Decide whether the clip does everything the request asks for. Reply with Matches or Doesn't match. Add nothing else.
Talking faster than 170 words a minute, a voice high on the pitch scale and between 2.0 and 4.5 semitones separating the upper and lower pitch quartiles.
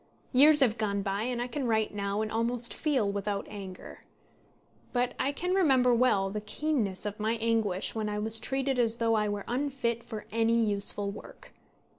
Matches